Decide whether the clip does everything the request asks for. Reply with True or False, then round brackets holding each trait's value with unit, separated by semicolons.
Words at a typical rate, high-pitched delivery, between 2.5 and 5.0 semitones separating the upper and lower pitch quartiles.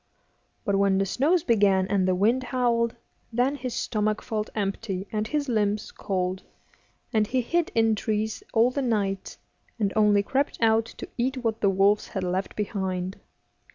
True (165 wpm; 215 Hz; 3.3 semitones)